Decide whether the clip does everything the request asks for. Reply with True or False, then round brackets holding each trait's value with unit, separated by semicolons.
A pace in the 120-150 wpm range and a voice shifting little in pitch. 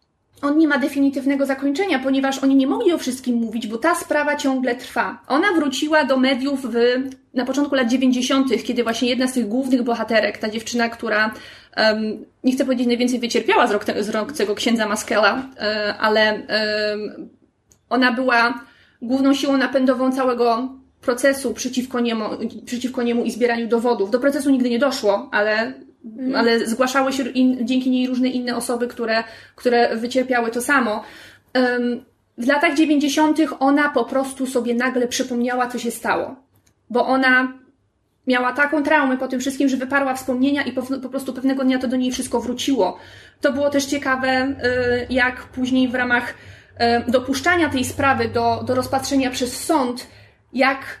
False (160 wpm; 2.3 semitones)